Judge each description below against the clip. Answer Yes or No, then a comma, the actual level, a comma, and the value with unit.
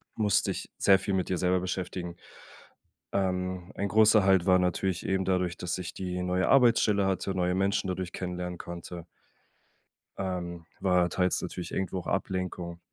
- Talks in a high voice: No, very low, 90 Hz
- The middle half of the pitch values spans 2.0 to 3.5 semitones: No, narrow, 1.2 semitones